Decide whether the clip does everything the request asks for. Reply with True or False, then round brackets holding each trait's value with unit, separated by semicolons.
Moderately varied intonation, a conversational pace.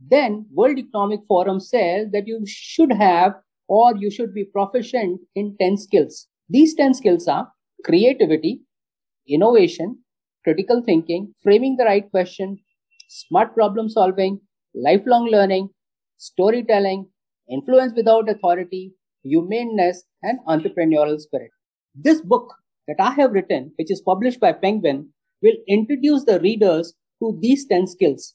True (4.7 semitones; 130 wpm)